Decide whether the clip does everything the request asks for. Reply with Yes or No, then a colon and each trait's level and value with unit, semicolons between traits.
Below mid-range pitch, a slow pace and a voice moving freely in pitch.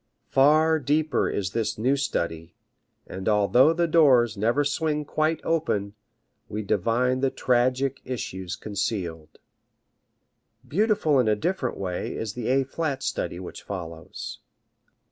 Yes: low, 125 Hz; slow, 125 wpm; wide, 6.6 semitones